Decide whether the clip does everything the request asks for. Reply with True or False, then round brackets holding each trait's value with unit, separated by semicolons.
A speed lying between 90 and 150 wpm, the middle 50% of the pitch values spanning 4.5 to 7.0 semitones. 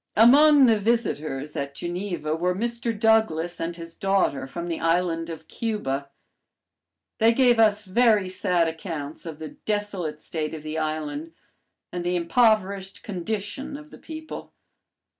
True (140 wpm; 5.5 semitones)